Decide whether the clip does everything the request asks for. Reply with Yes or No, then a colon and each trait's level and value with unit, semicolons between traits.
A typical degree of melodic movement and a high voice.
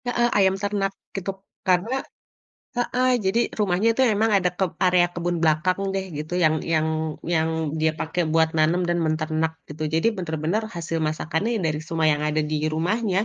No: average, 3.7 semitones; medium, 175 Hz